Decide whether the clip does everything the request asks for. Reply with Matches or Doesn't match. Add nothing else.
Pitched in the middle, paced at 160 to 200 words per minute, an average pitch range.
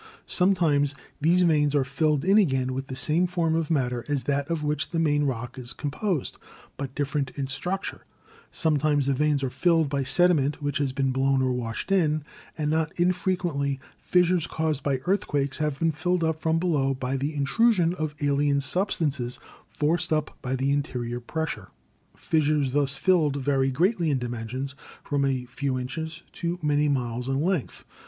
Matches